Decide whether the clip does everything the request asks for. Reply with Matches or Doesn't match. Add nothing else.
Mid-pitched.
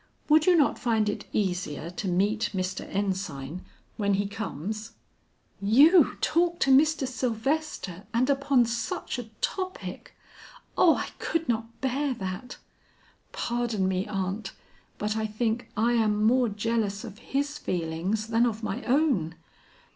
Doesn't match